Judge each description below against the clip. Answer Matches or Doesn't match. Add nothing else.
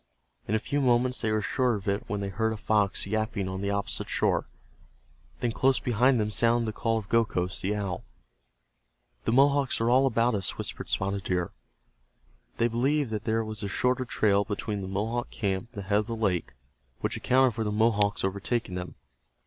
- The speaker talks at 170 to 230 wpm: Matches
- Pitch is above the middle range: Doesn't match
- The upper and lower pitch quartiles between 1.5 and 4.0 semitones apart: Matches